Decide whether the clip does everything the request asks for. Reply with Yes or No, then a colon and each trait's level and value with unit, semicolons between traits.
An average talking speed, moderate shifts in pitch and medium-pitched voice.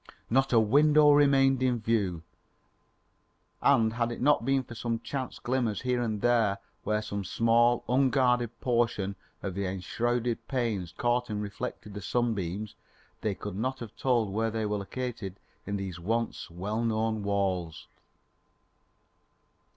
No: average, 145 wpm; average, 3.3 semitones; low, 115 Hz